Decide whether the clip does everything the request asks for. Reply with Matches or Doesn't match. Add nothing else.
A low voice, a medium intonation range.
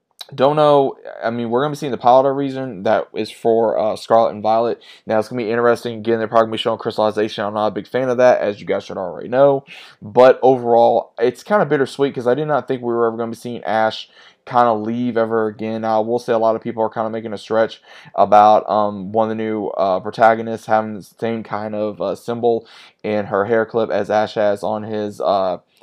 Doesn't match